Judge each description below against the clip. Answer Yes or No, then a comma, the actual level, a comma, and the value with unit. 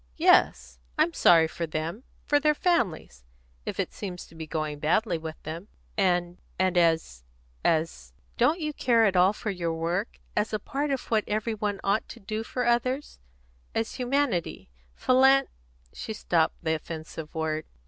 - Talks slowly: No, average, 170 wpm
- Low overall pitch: No, medium, 180 Hz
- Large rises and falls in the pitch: Yes, wide, 6.1 semitones